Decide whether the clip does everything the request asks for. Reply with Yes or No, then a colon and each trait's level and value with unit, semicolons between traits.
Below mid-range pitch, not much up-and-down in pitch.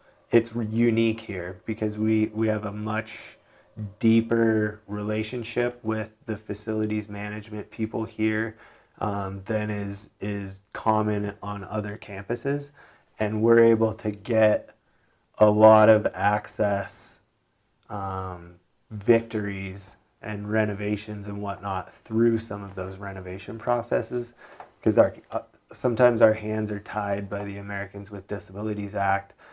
Yes: low, 105 Hz; narrow, 1.7 semitones